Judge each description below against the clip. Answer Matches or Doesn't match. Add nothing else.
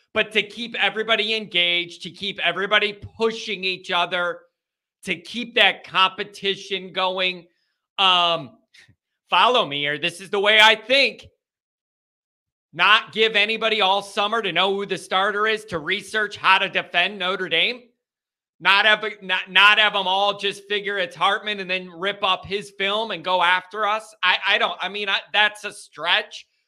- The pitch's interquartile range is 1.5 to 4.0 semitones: Matches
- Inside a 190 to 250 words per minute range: Doesn't match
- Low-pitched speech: Doesn't match